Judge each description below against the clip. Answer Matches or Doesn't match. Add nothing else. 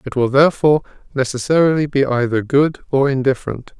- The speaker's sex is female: Doesn't match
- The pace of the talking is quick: Doesn't match